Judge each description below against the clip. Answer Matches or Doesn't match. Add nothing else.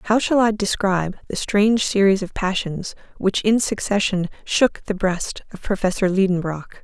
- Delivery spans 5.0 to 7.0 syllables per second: Doesn't match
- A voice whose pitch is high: Matches